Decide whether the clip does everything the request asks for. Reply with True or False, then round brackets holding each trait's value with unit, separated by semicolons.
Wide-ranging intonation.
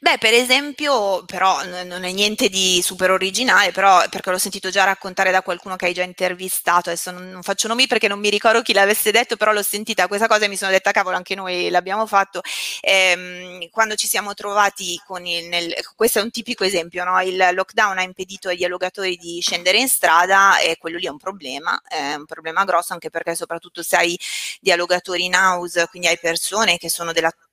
False (2.4 semitones)